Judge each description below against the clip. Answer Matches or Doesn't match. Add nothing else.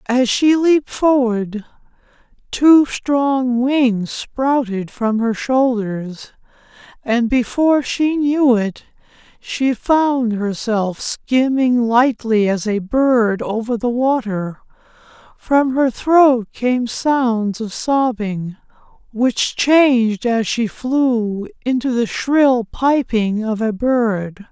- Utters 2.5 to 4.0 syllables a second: Matches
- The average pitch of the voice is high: Matches